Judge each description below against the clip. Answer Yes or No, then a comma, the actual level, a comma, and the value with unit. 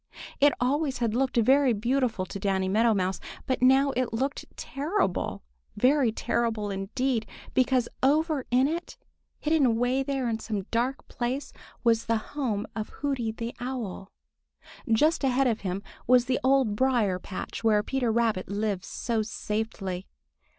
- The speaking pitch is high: Yes, high, 240 Hz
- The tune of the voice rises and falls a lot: No, average, 3.8 semitones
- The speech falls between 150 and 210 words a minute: No, average, 140 wpm